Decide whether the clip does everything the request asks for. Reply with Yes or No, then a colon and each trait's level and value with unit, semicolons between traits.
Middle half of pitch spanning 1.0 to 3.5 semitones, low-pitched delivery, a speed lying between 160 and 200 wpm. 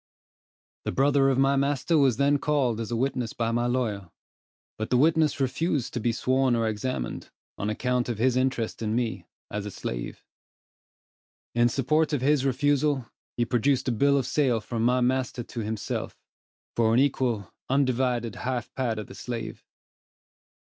Yes: average, 2.9 semitones; low, 125 Hz; average, 170 wpm